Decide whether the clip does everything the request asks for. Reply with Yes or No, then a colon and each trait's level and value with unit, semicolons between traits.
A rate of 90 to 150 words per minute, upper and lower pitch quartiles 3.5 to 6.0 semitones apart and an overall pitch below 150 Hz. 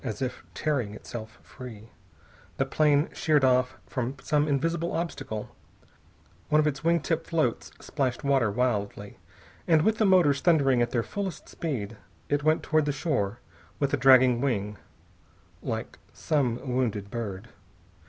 Yes: average, 145 wpm; average, 4.6 semitones; low, 135 Hz